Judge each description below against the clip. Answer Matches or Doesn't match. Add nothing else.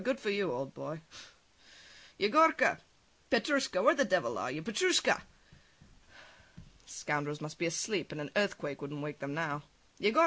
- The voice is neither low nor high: Matches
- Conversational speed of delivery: Matches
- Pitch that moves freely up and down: Matches